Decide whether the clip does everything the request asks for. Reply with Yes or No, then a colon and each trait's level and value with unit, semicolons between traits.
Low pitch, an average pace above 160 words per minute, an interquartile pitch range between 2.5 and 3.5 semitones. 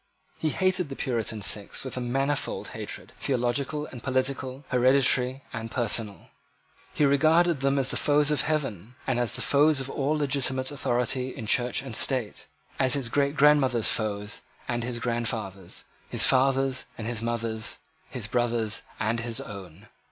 No: low, 130 Hz; average, 155 wpm; average, 3.1 semitones